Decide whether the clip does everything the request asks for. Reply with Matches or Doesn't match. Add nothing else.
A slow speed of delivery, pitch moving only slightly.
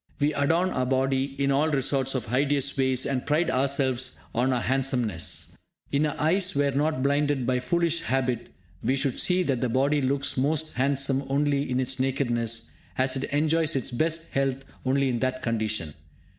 Doesn't match